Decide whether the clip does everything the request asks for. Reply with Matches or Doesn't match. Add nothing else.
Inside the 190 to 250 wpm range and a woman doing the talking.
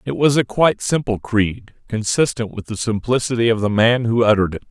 Doesn't match